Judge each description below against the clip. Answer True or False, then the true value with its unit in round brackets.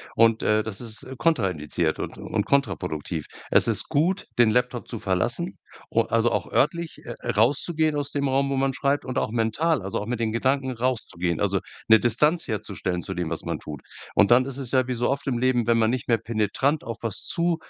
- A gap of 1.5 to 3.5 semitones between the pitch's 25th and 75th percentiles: False (4.3 semitones)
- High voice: False (120 Hz)